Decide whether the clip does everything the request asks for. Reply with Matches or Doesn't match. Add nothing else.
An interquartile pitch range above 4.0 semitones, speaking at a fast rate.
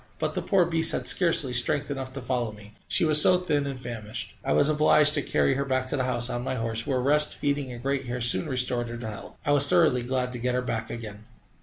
Doesn't match